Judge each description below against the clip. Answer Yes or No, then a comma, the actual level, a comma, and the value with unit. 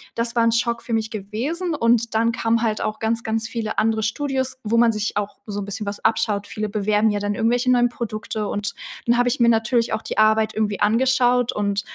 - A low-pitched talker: No, high, 225 Hz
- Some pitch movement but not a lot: No, narrow, 1.9 semitones